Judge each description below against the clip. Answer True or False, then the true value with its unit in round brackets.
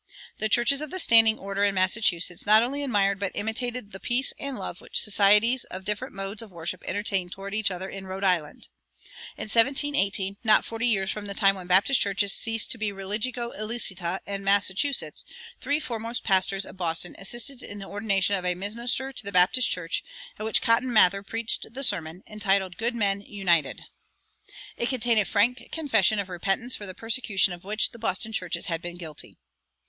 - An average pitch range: True (3.3 semitones)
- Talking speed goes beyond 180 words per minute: True (190 wpm)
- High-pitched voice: True (205 Hz)